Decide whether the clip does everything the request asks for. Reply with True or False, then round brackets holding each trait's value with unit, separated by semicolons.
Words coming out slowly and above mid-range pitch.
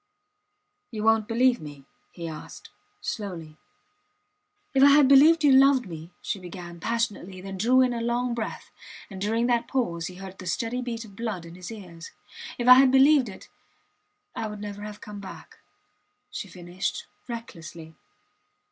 False (165 wpm; 210 Hz)